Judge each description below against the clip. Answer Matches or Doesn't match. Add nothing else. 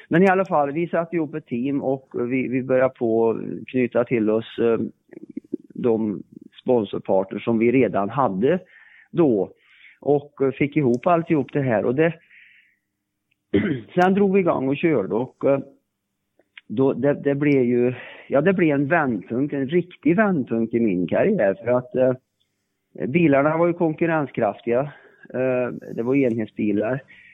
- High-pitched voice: Doesn't match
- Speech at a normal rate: Matches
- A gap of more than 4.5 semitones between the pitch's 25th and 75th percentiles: Matches